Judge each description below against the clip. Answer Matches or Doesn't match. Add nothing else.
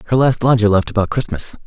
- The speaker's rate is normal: Doesn't match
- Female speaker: Doesn't match